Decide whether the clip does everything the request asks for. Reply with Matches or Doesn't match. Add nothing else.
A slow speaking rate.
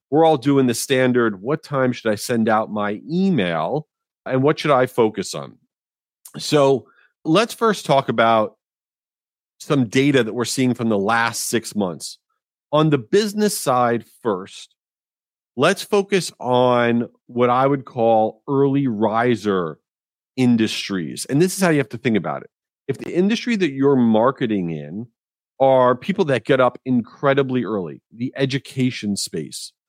Doesn't match